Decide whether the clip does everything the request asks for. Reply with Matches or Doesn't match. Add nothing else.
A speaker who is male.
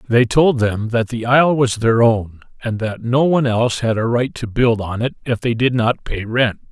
Matches